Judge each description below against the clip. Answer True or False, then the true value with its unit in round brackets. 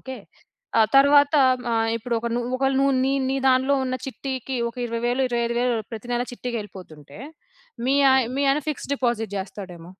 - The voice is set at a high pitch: True (245 Hz)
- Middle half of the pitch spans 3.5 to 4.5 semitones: False (2.9 semitones)